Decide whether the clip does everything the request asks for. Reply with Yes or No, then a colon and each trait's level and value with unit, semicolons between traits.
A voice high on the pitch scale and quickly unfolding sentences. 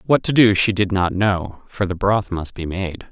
No: very low, 95 Hz; fast, 250 wpm